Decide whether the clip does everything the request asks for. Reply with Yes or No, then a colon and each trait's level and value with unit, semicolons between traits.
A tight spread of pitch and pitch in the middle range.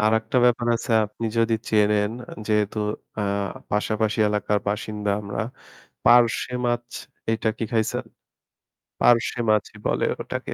No: narrow, 1.7 semitones; low, 110 Hz